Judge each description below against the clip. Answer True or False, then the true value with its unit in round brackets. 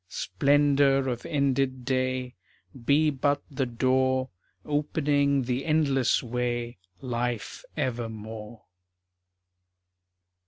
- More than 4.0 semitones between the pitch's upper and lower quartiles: False (2.6 semitones)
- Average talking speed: False (80 wpm)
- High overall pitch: False (130 Hz)